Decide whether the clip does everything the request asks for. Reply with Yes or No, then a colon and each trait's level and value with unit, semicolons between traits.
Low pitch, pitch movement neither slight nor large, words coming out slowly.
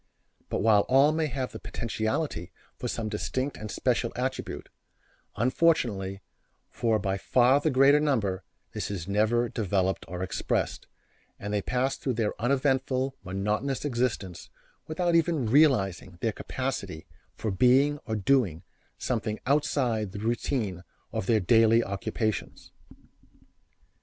Yes: low, 115 Hz; average, 4.8 semitones; slow, 125 wpm